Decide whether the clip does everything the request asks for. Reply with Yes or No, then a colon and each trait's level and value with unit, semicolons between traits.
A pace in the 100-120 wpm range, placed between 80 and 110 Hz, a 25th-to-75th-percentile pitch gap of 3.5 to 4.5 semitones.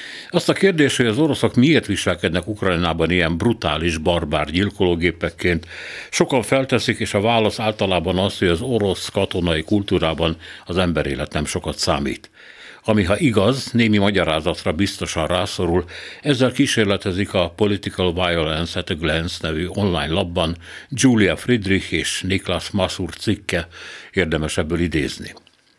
No: average, 135 wpm; very low, 95 Hz; average, 4.2 semitones